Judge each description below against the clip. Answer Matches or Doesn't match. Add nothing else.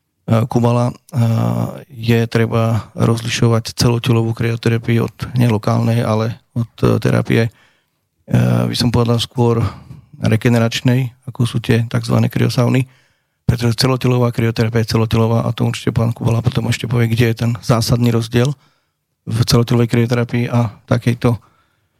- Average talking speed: Matches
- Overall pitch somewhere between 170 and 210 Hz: Doesn't match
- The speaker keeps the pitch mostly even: Matches